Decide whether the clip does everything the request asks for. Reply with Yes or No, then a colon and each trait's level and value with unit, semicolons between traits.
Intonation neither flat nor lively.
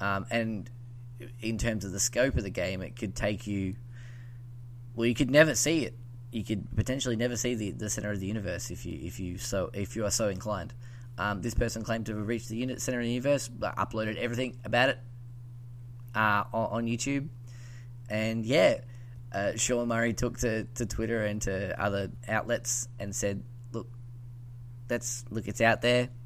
No: narrow, 2.0 semitones